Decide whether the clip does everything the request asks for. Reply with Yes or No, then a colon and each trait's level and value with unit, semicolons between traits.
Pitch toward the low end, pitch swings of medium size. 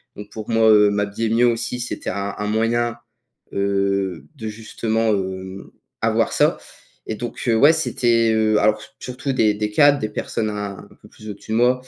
No: low, 110 Hz; narrow, 2.3 semitones